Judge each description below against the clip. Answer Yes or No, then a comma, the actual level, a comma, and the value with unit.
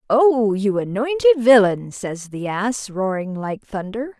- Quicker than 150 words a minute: No, average, 145 wpm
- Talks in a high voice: Yes, high, 220 Hz